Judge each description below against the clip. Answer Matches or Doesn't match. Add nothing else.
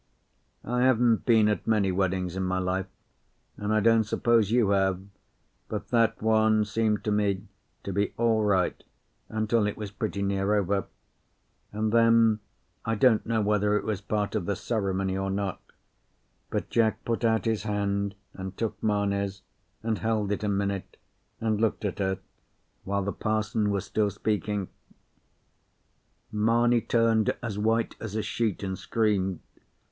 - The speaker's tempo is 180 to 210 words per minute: Doesn't match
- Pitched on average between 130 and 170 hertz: Doesn't match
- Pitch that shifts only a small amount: Matches